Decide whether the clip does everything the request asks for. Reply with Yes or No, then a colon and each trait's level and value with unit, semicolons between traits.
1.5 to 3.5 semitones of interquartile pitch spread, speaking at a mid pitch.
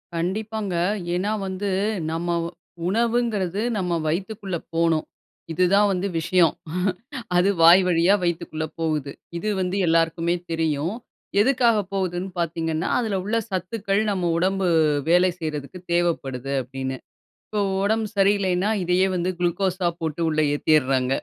Yes: average, 3.1 semitones; medium, 180 Hz